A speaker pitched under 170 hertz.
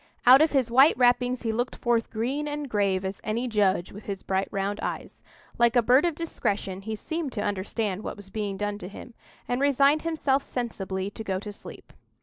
No: high, 225 Hz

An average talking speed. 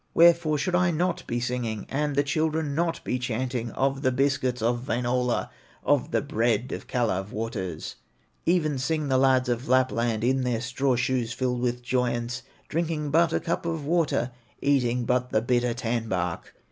Yes: average, 170 wpm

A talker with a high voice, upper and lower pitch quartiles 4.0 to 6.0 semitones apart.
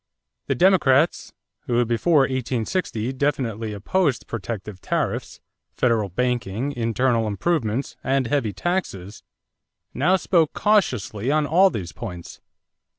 No: low, 125 Hz; average, 5.1 semitones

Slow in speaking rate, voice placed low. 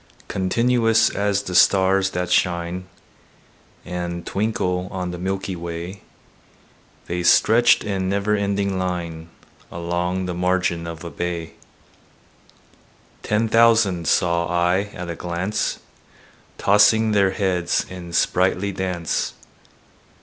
Yes: slow, 110 wpm; very low, 90 Hz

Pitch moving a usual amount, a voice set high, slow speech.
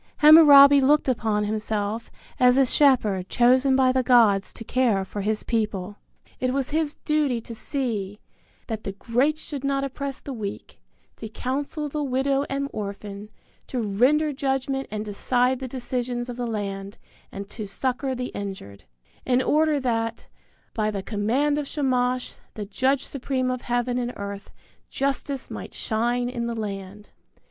No: average, 4.2 semitones; high, 245 Hz; average, 155 wpm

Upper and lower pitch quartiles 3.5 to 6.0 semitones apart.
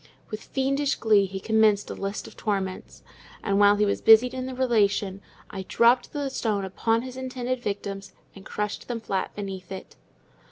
Yes: average, 3.9 semitones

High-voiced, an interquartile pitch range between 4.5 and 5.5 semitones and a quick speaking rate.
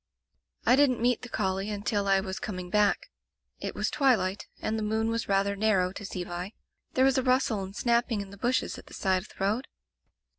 No: high, 210 Hz; average, 3.6 semitones; fast, 220 wpm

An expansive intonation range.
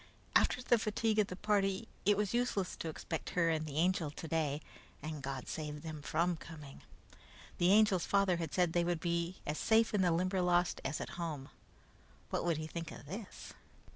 No: average, 3.8 semitones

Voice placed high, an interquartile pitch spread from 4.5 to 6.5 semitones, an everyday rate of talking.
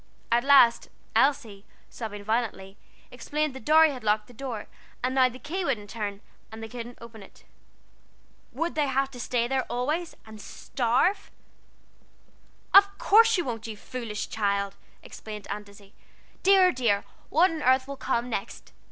Yes: high, 245 Hz; average, 4.9 semitones; average, 160 wpm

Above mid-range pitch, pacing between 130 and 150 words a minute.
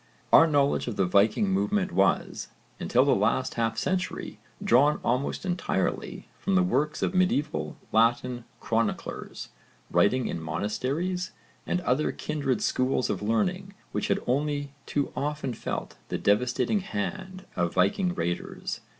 No: medium, 140 Hz; slow, 135 wpm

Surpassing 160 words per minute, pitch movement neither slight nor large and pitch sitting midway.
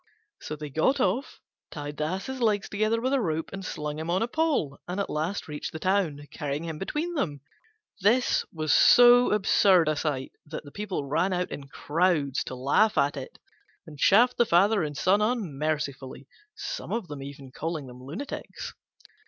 No: average, 175 wpm; wide, 6.3 semitones; medium, 165 Hz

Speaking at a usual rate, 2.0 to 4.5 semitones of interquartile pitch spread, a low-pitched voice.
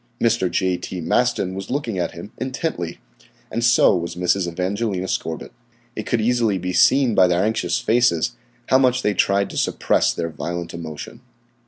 No: average, 170 wpm; average, 5.1 semitones; very low, 95 Hz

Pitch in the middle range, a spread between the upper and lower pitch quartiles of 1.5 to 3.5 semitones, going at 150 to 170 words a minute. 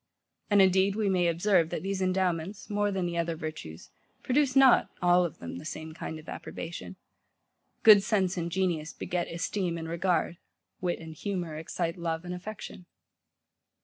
Yes: medium, 180 Hz; average, 2.7 semitones; average, 165 wpm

